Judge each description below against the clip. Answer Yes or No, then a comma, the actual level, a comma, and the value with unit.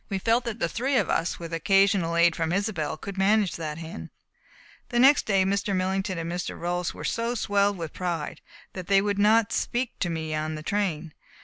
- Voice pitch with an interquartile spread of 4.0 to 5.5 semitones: No, average, 3.6 semitones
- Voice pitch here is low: No, high, 190 Hz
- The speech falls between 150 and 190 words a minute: No, fast, 205 wpm